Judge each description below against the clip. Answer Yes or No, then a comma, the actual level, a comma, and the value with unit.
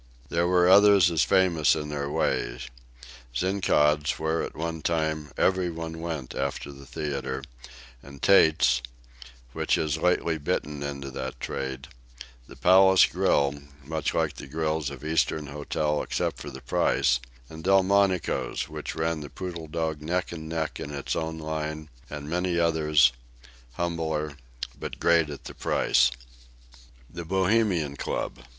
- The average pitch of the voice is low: Yes, very low, 80 Hz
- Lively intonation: No, average, 2.8 semitones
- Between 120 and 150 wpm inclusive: Yes, average, 140 wpm